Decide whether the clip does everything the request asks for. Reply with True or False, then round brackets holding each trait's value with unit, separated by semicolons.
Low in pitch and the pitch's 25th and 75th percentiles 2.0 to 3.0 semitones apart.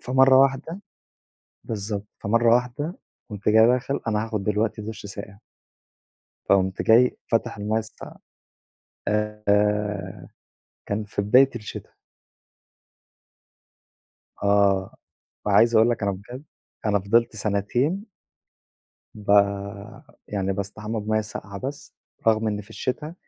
True (105 Hz; 2.7 semitones)